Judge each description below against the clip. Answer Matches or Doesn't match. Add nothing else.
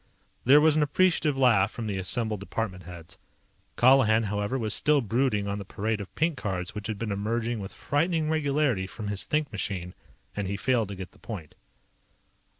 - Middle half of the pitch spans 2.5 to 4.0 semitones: Doesn't match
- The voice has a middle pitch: Doesn't match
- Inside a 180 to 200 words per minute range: Matches